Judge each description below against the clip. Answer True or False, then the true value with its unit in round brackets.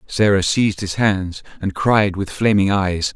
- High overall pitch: False (100 Hz)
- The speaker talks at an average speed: True (170 wpm)